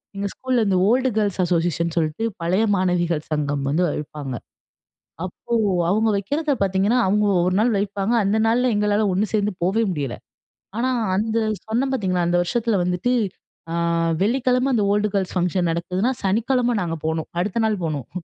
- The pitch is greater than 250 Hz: No, high, 200 Hz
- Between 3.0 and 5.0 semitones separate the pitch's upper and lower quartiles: Yes, average, 4.4 semitones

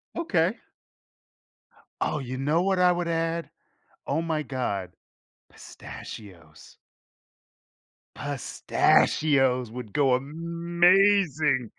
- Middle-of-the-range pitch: Yes, medium, 150 Hz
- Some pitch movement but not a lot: Yes, average, 4.9 semitones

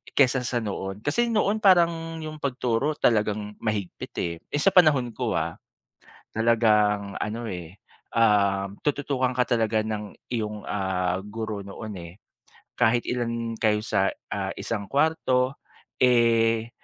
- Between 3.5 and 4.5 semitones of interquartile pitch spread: Yes, average, 3.8 semitones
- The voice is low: Yes, low, 115 Hz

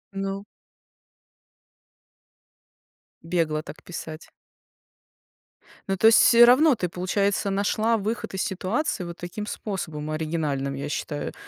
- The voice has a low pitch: No, high, 190 Hz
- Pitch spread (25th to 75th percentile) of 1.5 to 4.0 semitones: No, average, 4.9 semitones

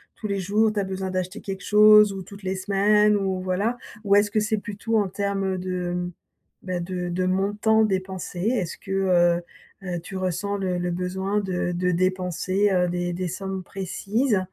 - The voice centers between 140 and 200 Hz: Yes, high, 190 Hz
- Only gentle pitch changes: Yes, narrow, 1.9 semitones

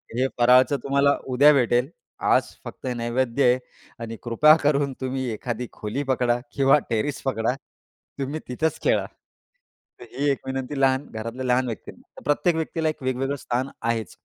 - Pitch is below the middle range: Yes, low, 130 Hz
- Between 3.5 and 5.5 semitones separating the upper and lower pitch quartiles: No, average, 2.7 semitones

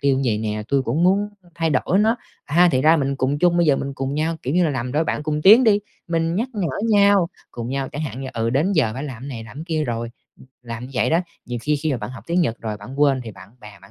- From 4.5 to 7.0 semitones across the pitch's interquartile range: Yes, average, 5.2 semitones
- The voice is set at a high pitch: No, medium, 140 Hz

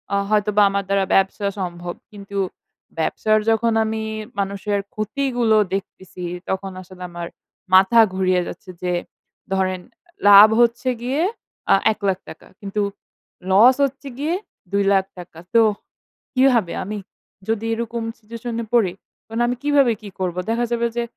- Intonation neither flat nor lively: Yes, average, 3.5 semitones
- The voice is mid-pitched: No, high, 210 Hz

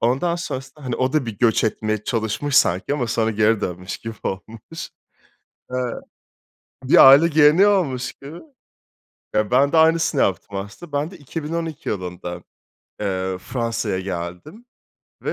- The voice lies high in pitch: No, low, 125 Hz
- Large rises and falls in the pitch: Yes, wide, 6.6 semitones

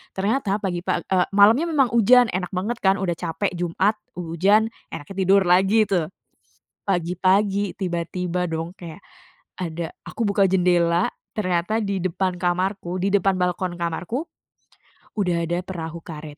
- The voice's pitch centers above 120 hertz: Yes, medium, 185 Hz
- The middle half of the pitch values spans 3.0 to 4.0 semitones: No, narrow, 2.6 semitones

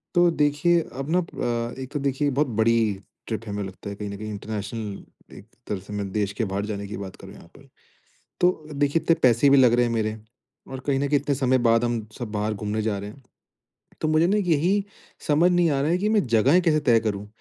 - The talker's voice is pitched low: Yes, low, 120 Hz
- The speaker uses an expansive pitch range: Yes, wide, 6.0 semitones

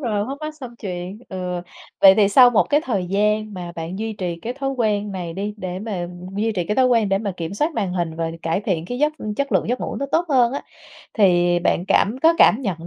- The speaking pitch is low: No, high, 205 Hz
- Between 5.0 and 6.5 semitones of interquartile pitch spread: Yes, average, 5.3 semitones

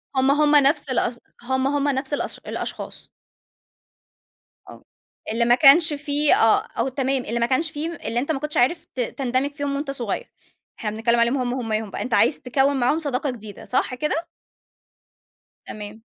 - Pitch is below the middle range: No, very high, 265 Hz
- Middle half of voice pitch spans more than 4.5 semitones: No, average, 3.2 semitones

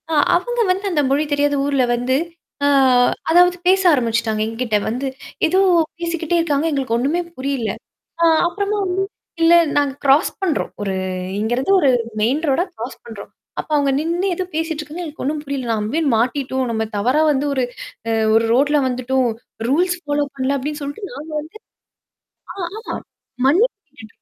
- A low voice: No, very high, 285 Hz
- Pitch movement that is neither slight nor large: Yes, average, 4.4 semitones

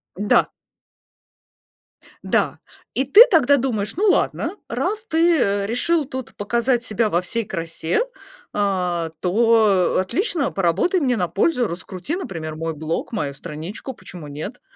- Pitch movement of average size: No, wide, 7.1 semitones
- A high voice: Yes, high, 210 Hz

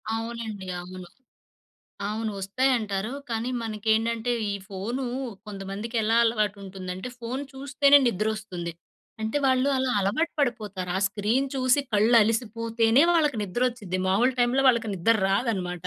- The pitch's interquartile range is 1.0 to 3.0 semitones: No, average, 3.7 semitones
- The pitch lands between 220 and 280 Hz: Yes, high, 225 Hz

